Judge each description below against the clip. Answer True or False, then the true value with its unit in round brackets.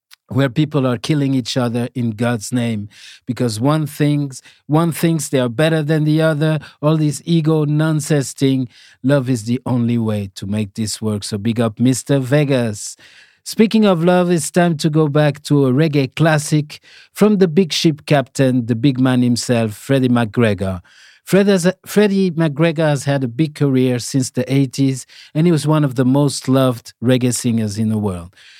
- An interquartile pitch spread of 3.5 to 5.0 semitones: True (4.3 semitones)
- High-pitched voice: False (135 Hz)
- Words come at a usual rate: True (180 wpm)